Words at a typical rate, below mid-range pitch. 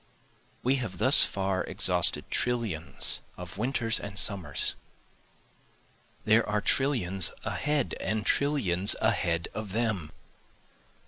No: slow, 105 wpm; low, 105 Hz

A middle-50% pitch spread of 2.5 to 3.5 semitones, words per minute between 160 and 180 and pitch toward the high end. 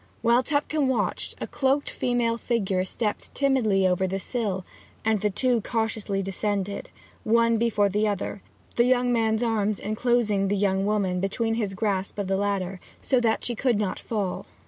Yes: average, 3.2 semitones; average, 170 wpm; high, 215 Hz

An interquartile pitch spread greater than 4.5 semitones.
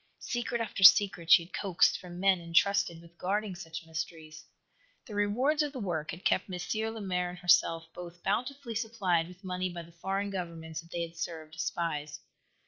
No: average, 3.2 semitones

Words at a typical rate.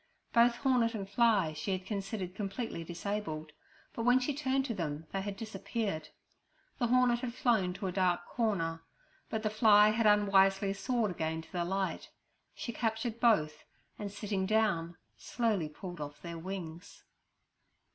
Yes: average, 155 wpm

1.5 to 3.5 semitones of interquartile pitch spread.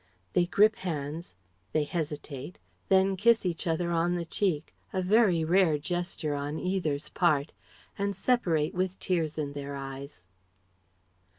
No: average, 3.9 semitones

